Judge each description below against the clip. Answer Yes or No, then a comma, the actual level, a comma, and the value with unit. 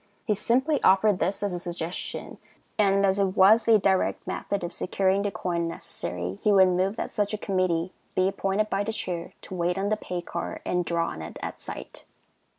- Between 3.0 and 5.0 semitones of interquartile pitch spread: No, narrow, 2.6 semitones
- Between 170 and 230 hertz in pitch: Yes, high, 190 Hz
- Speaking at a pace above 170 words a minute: Yes, fast, 205 wpm